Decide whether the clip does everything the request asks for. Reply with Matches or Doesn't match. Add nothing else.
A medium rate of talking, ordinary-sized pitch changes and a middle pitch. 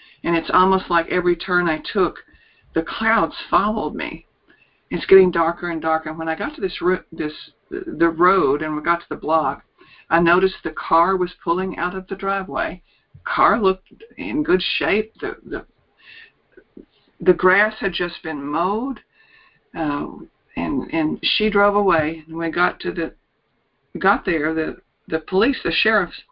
Matches